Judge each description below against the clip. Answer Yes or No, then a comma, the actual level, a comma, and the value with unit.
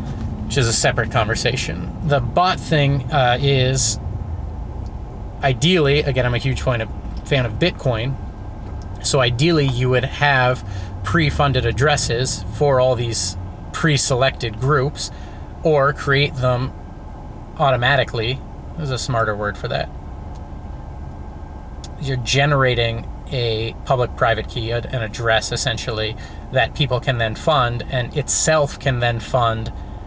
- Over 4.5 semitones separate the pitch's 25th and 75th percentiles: Yes, average, 5.3 semitones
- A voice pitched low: Yes, low, 120 Hz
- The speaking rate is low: Yes, slow, 115 wpm